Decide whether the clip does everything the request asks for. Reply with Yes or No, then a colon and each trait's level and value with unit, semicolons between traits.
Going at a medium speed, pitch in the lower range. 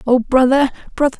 No: average, 150 wpm; very high, 260 Hz